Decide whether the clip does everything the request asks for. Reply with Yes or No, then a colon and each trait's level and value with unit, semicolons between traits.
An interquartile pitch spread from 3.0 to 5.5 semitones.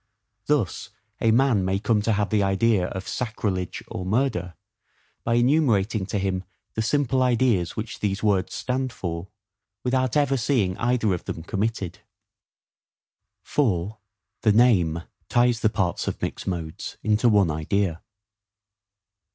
Yes: average, 4.4 semitones